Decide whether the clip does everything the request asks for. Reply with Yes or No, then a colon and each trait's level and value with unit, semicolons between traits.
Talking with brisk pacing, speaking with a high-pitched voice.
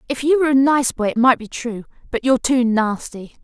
Yes: fast, 225 wpm; very high, 250 Hz